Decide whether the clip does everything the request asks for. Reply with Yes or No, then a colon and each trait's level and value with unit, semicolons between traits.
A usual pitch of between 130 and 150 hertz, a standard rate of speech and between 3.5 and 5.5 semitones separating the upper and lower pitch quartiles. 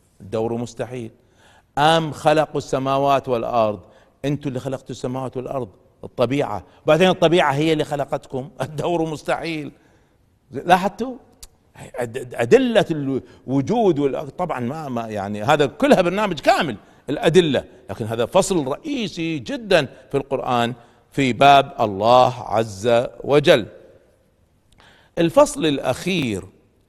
Yes: low, 135 Hz; average, 100 wpm; average, 5.1 semitones